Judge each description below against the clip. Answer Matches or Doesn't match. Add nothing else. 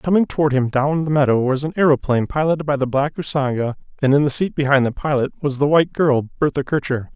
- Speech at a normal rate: Doesn't match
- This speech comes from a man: Matches